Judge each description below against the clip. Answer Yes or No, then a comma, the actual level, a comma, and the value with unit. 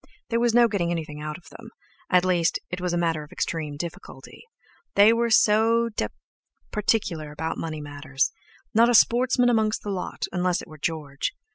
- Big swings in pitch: Yes, wide, 6.2 semitones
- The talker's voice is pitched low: No, medium, 180 Hz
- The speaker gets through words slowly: No, average, 180 wpm